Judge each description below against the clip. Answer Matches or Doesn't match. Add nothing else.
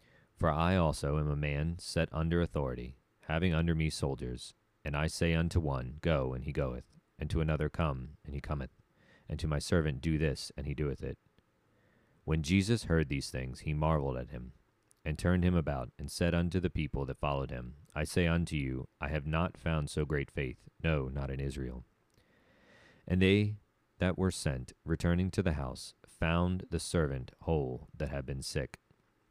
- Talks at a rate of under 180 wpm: Doesn't match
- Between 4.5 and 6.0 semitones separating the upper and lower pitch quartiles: Doesn't match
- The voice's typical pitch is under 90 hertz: Matches